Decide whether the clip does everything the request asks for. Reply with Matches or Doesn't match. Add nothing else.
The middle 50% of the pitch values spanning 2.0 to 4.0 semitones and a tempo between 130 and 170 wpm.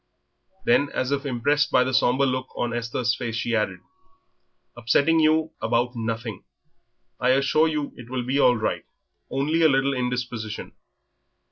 Matches